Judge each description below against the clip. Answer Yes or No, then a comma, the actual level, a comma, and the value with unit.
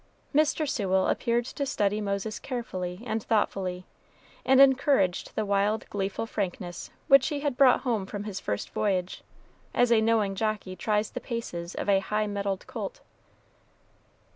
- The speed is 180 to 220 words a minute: No, average, 150 wpm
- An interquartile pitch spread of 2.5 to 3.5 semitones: No, average, 3.9 semitones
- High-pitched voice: Yes, high, 210 Hz